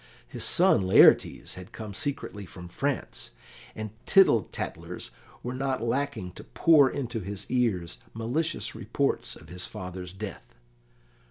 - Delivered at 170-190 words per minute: No, slow, 135 wpm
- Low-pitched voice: Yes, low, 115 Hz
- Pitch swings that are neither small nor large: No, wide, 6.4 semitones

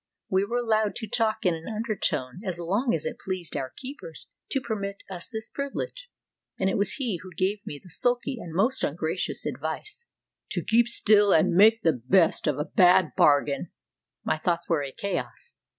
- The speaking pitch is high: Yes, high, 195 Hz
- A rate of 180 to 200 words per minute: Yes, average, 185 wpm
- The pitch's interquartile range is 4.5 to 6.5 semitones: Yes, wide, 5.6 semitones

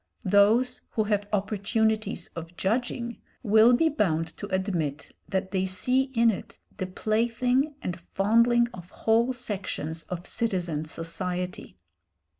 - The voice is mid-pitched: No, high, 205 Hz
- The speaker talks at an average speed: No, slow, 125 wpm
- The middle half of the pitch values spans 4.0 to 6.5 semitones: Yes, average, 4.3 semitones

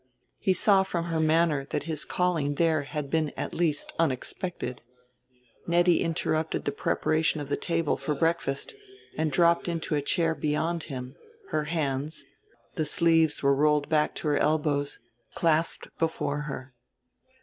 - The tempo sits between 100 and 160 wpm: Yes, average, 150 wpm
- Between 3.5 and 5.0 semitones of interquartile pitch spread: No, narrow, 2.4 semitones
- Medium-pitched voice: Yes, medium, 155 Hz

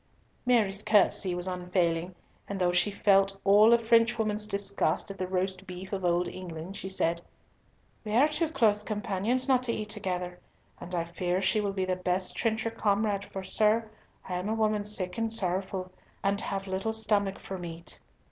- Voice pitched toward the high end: Yes, high, 195 Hz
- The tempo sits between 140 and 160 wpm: No, average, 180 wpm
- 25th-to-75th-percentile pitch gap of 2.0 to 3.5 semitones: Yes, average, 2.8 semitones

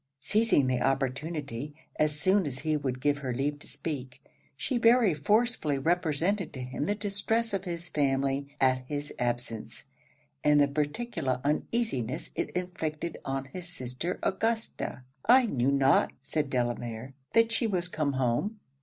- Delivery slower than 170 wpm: Yes, average, 150 wpm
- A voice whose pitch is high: No, medium, 150 Hz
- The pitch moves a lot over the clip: Yes, wide, 5.7 semitones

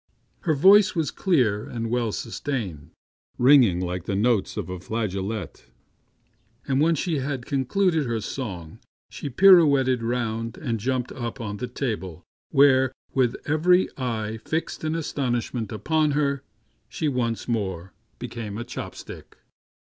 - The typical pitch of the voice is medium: No, low, 125 Hz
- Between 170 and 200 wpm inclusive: No, average, 140 wpm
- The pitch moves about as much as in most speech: Yes, average, 4.7 semitones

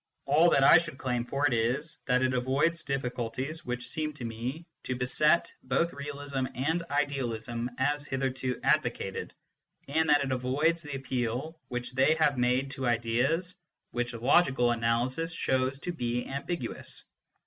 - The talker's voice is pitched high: No, low, 130 Hz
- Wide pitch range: No, average, 3.3 semitones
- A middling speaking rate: Yes, average, 150 wpm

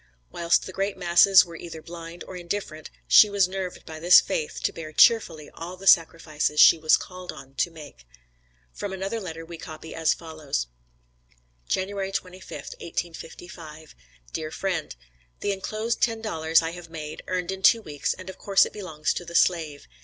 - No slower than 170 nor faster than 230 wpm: Yes, average, 175 wpm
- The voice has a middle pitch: Yes, medium, 170 Hz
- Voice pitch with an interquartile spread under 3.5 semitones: Yes, average, 3.1 semitones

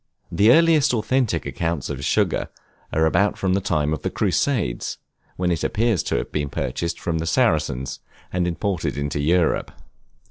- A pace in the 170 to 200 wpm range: No, average, 155 wpm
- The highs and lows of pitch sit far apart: Yes, wide, 5.7 semitones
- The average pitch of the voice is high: No, very low, 85 Hz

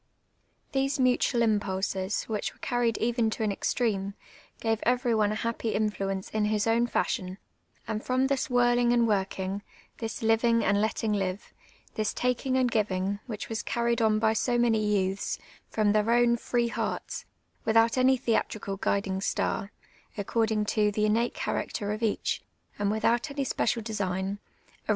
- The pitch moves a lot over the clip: No, narrow, 2.6 semitones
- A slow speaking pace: No, average, 165 wpm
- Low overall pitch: No, high, 220 Hz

